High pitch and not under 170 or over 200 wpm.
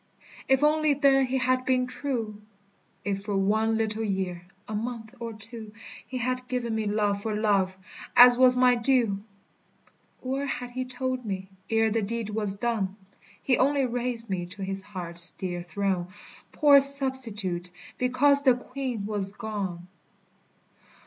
No: high, 225 Hz; average, 150 wpm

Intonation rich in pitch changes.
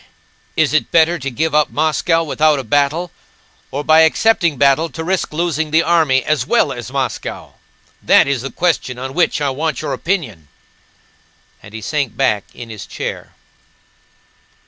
No: average, 3.6 semitones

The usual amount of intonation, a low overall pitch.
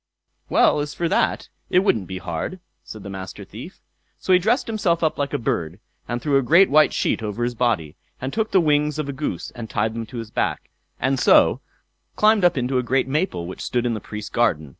No: wide, 6.7 semitones; low, 130 Hz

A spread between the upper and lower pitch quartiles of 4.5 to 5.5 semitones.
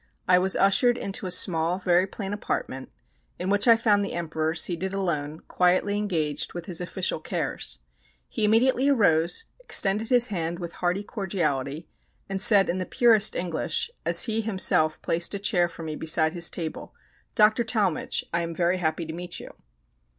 No: average, 3.7 semitones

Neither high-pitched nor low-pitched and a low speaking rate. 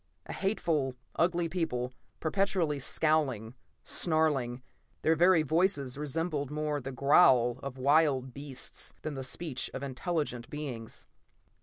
Yes: medium, 145 Hz; slow, 120 wpm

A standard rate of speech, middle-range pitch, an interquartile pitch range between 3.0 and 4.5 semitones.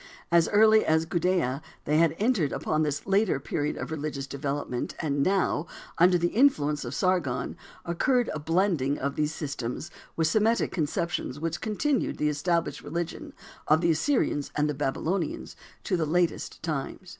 Yes: average, 155 wpm; medium, 160 Hz; average, 3.9 semitones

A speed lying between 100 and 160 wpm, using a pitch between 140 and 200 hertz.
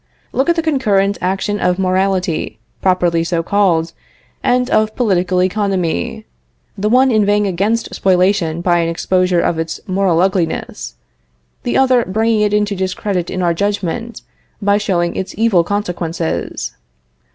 Yes: average, 140 wpm; high, 190 Hz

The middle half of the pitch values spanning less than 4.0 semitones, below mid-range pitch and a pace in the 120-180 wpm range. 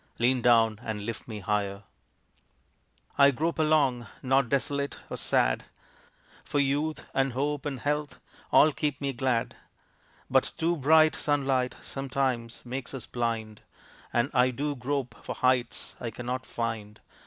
Yes: average, 3.3 semitones; low, 130 Hz; average, 140 wpm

